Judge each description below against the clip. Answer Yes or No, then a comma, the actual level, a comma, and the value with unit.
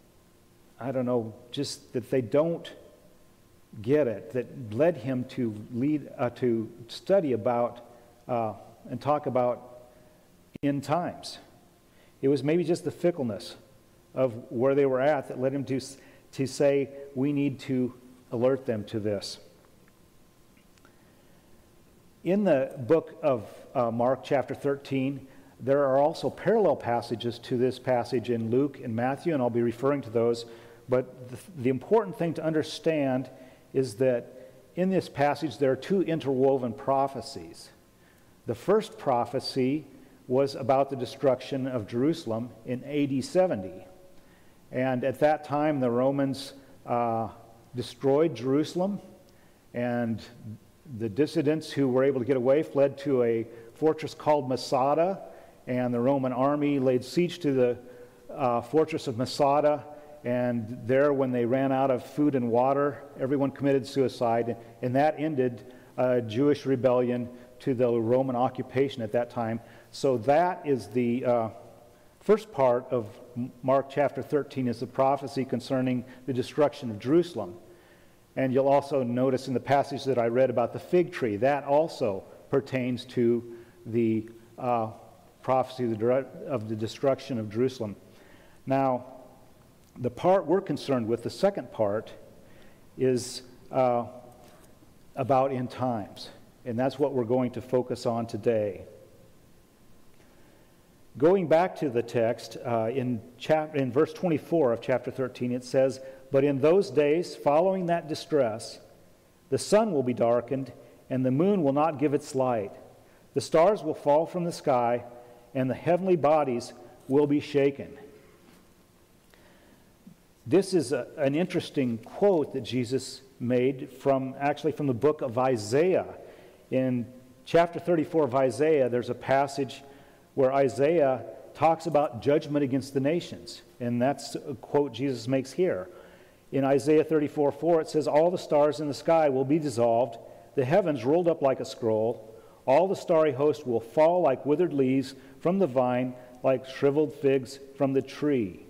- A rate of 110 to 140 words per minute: No, average, 150 wpm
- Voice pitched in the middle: No, low, 130 Hz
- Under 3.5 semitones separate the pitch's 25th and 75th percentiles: Yes, average, 2.9 semitones